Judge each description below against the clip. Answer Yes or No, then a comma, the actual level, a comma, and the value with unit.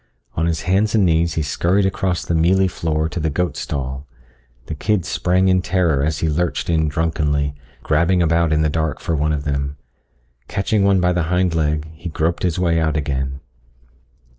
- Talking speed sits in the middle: Yes, average, 190 wpm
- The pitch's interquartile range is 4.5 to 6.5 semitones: No, average, 2.9 semitones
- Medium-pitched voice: No, very low, 80 Hz